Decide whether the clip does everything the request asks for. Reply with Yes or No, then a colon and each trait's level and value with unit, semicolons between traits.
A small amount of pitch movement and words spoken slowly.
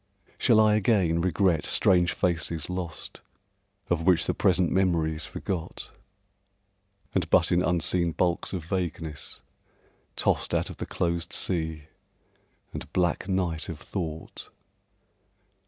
Yes: narrow, 2.2 semitones; slow, 120 wpm